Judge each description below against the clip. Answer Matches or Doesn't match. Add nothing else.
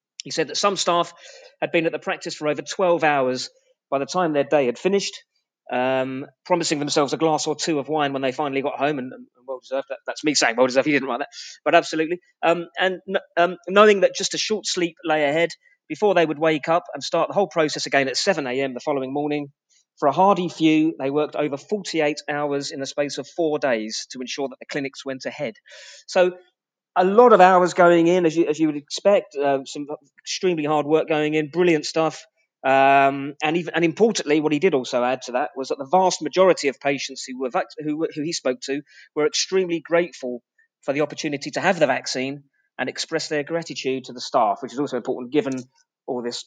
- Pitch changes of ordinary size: Matches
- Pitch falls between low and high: Matches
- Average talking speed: Doesn't match